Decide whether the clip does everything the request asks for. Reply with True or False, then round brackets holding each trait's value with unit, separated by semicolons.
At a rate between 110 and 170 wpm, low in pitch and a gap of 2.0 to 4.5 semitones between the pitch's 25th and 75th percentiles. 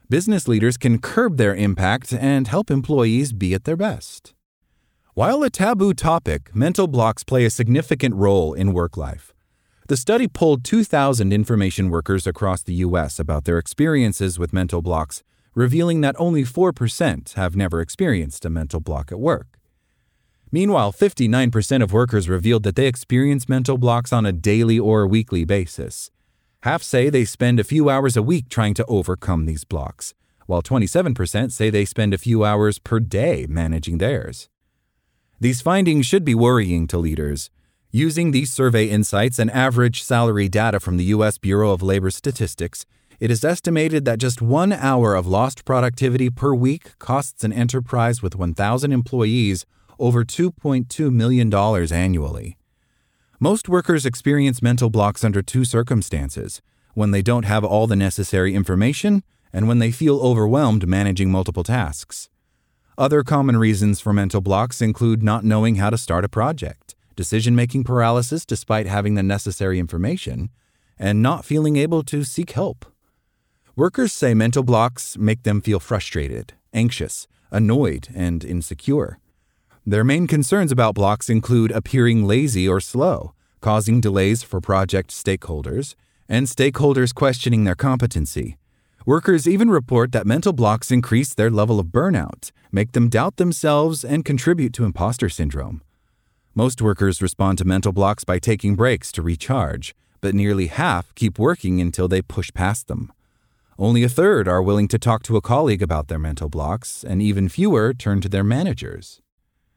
False (155 wpm; 110 Hz; 5.1 semitones)